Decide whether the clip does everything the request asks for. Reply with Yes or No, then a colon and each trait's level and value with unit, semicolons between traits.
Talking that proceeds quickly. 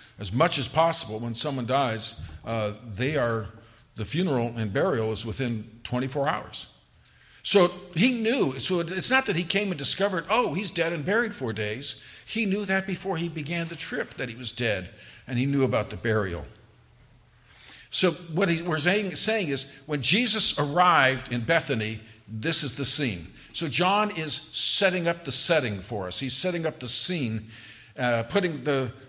No: average, 175 wpm